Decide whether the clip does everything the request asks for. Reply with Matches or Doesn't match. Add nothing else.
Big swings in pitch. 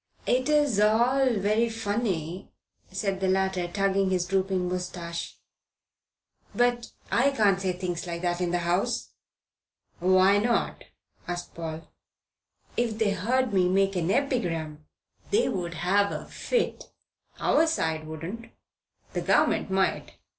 Doesn't match